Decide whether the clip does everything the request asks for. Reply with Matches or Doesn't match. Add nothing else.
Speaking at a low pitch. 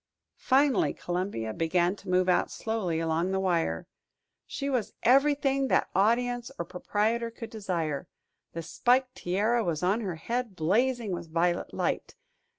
Doesn't match